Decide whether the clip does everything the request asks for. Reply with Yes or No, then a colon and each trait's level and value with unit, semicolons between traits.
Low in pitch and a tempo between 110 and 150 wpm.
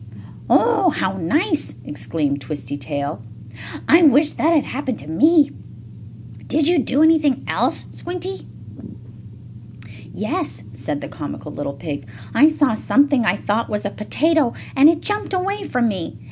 No: very high, 275 Hz; average, 145 wpm